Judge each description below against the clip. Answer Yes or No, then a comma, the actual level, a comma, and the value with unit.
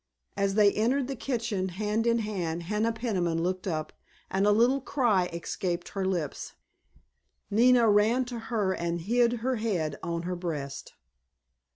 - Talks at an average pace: Yes, average, 155 wpm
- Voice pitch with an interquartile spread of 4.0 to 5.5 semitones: Yes, average, 4.9 semitones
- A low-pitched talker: No, high, 205 Hz